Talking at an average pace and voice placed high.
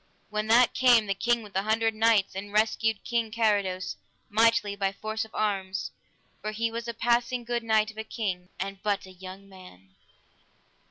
Yes: average, 180 wpm; high, 215 Hz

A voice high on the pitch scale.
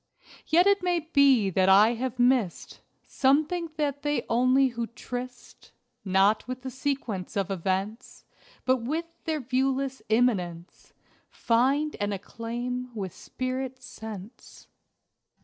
Yes: very high, 250 Hz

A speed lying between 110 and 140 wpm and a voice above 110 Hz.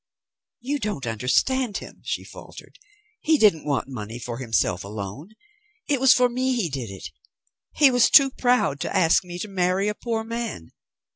No: average, 170 wpm; high, 190 Hz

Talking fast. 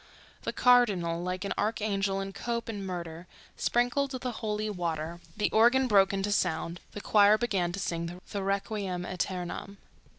No: average, 155 wpm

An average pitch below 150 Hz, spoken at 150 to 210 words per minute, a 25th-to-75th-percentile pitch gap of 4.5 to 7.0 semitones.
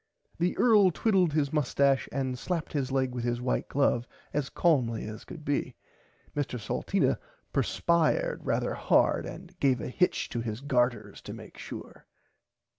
Yes: medium, 140 Hz; average, 155 wpm; average, 5.3 semitones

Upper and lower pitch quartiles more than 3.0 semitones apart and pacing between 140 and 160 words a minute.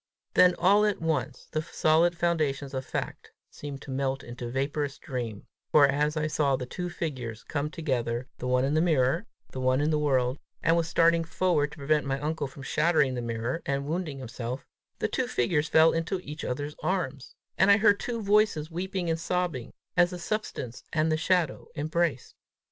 No: average, 4.1 semitones; average, 190 wpm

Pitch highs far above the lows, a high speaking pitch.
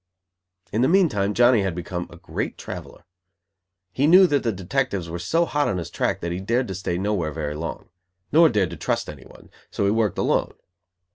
No: wide, 6.9 semitones; low, 100 Hz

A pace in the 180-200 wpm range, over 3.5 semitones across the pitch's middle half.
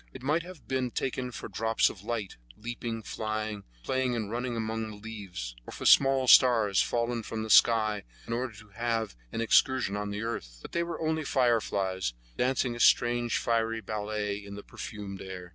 No: average, 185 wpm; average, 3.0 semitones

